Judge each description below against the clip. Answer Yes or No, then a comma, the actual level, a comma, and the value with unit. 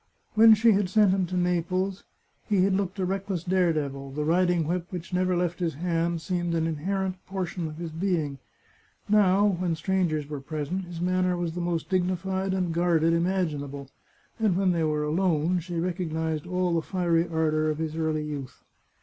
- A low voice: No, medium, 175 Hz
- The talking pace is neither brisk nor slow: Yes, average, 180 wpm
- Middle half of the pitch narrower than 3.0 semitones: Yes, narrow, 2.6 semitones